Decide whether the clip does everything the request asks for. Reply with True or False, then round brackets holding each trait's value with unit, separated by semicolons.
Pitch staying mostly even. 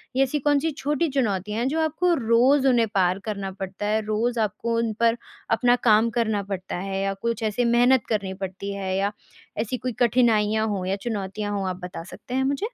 False (3.9 semitones)